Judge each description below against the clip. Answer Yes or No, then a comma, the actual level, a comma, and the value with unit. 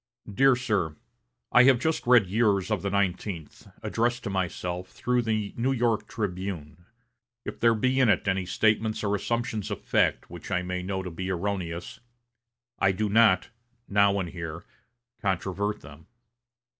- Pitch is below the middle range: Yes, low, 100 Hz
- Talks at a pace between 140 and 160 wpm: Yes, average, 155 wpm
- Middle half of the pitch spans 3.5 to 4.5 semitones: Yes, average, 3.8 semitones